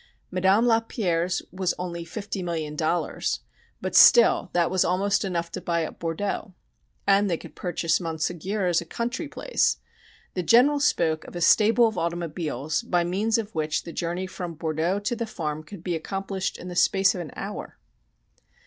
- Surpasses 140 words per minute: Yes, average, 175 wpm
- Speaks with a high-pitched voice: No, medium, 180 Hz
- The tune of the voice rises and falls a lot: No, average, 3.3 semitones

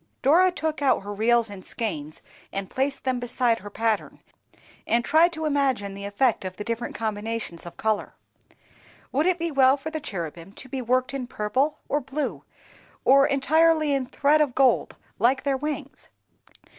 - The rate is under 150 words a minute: No, average, 170 wpm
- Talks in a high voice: Yes, very high, 255 Hz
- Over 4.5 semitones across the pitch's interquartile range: Yes, average, 5.1 semitones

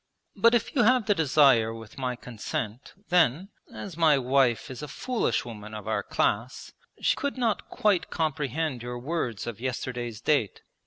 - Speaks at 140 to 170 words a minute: Yes, average, 165 wpm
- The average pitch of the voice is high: No, low, 135 Hz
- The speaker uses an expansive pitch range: Yes, wide, 6.2 semitones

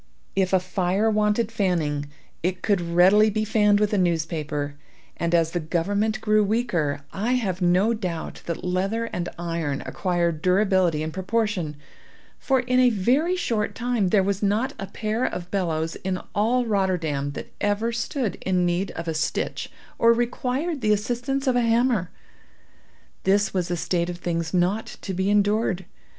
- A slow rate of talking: No, average, 165 wpm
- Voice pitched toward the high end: Yes, high, 195 Hz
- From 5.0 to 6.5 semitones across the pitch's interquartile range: No, average, 4.2 semitones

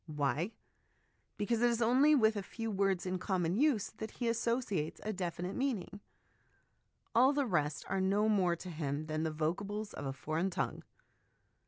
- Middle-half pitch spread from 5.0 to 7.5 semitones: Yes, average, 5.3 semitones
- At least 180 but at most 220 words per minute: No, average, 170 wpm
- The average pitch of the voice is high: Yes, high, 195 Hz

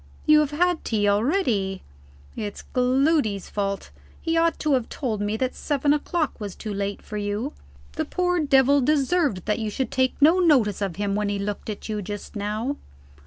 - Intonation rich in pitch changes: Yes, wide, 6.4 semitones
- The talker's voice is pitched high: Yes, high, 245 Hz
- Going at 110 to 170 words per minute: No, average, 185 wpm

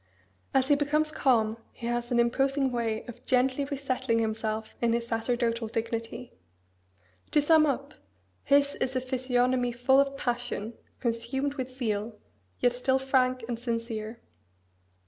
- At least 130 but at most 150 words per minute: Yes, average, 140 wpm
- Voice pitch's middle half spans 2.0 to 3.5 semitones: Yes, narrow, 2.5 semitones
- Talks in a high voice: Yes, high, 245 Hz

